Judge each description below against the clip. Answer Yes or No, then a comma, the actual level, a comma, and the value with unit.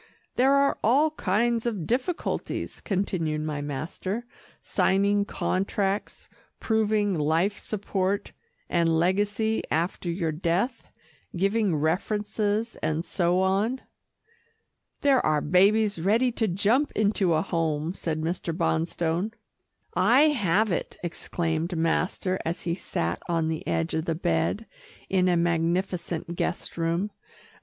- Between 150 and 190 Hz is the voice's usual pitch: Yes, medium, 185 Hz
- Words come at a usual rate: No, slow, 120 wpm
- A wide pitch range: No, average, 4.2 semitones